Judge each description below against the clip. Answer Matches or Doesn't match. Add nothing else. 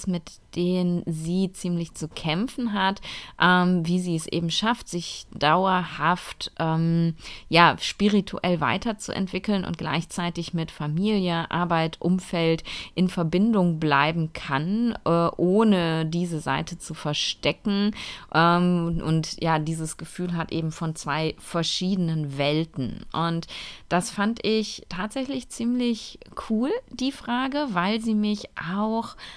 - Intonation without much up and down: Doesn't match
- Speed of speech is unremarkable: Doesn't match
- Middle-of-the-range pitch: Matches